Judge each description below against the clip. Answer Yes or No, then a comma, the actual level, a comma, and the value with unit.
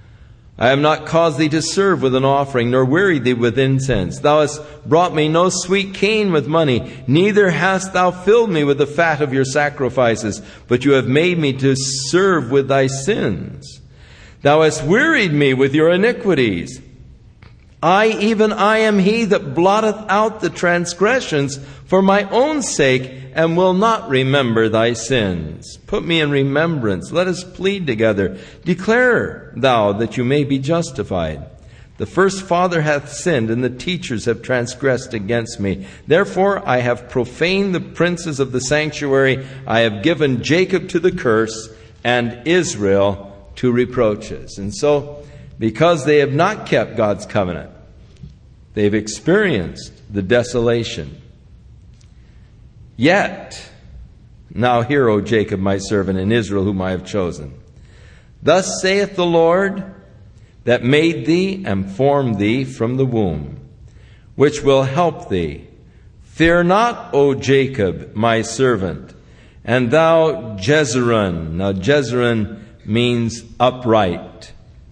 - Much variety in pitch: Yes, wide, 7.1 semitones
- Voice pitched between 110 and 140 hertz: Yes, low, 135 Hz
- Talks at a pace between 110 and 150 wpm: Yes, average, 140 wpm